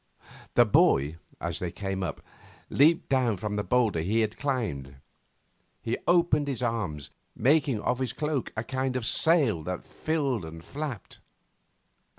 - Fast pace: No, average, 150 wpm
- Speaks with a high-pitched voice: No, low, 115 Hz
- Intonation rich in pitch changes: Yes, wide, 6.9 semitones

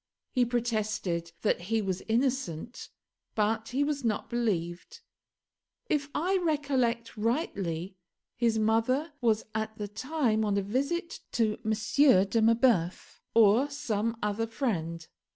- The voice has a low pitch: No, high, 225 Hz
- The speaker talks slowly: Yes, slow, 125 wpm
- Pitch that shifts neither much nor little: Yes, average, 3.9 semitones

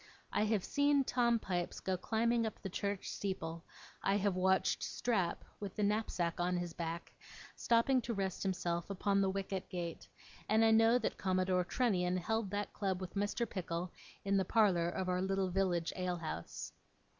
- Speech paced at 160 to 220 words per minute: Yes, average, 170 wpm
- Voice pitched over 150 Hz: Yes, high, 190 Hz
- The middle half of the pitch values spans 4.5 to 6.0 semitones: No, average, 3.2 semitones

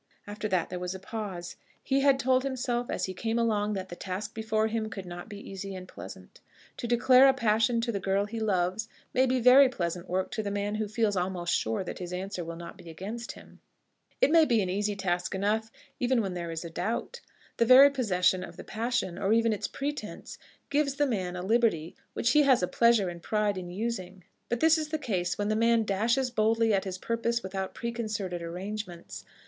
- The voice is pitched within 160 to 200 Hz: No, high, 210 Hz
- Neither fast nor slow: No, fast, 220 wpm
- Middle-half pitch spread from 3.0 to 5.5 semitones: Yes, average, 4.1 semitones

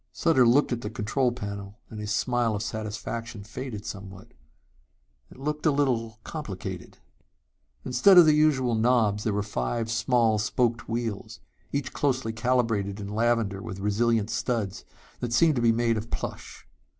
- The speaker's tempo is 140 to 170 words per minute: Yes, average, 155 wpm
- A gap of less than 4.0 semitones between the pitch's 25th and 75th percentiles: Yes, average, 3.0 semitones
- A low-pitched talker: Yes, low, 115 Hz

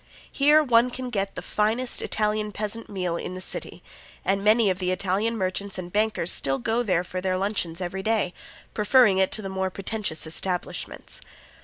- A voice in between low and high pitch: No, high, 200 Hz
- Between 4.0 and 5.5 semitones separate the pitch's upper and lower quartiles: No, average, 3.1 semitones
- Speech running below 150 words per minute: No, average, 180 wpm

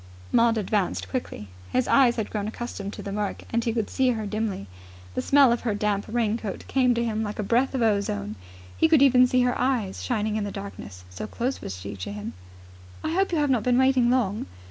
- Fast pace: Yes, fast, 220 wpm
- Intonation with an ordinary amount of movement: Yes, average, 3.8 semitones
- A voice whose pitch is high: Yes, high, 225 Hz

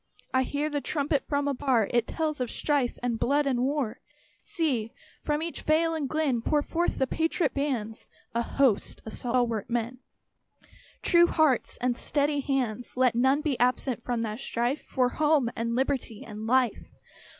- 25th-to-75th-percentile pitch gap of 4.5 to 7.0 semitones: No, average, 3.7 semitones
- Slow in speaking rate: No, average, 165 wpm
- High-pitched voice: Yes, very high, 260 Hz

